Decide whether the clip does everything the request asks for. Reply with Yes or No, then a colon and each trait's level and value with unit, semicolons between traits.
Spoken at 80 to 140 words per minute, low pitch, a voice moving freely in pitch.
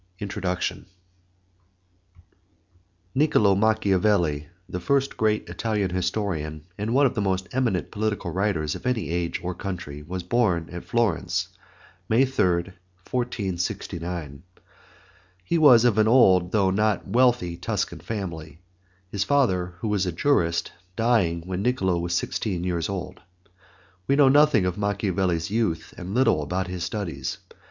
No: slow, 135 wpm; very low, 95 Hz; average, 4.1 semitones